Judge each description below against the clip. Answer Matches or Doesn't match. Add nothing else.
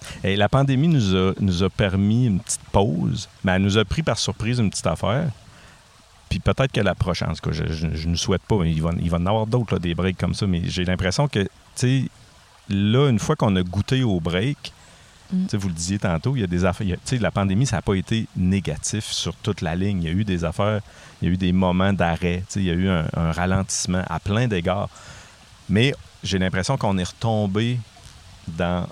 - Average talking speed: Doesn't match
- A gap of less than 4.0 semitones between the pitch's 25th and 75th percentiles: Matches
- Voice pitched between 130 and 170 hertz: Doesn't match